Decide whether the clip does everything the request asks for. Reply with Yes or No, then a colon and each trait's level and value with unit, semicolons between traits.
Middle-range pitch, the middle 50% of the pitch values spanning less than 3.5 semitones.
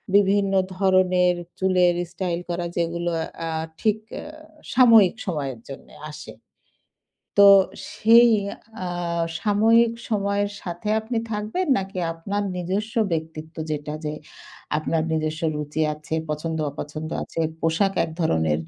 No: medium, 180 Hz; average, 4.3 semitones